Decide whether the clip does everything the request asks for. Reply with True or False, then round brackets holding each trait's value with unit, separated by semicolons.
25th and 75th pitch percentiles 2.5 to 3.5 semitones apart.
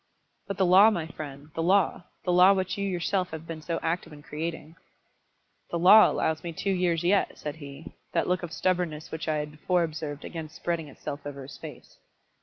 True (3.0 semitones)